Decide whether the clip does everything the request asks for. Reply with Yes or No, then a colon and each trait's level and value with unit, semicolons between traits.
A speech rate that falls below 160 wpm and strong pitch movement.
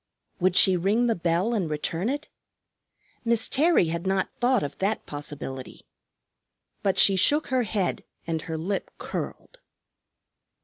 Yes: average, 140 wpm; wide, 5.8 semitones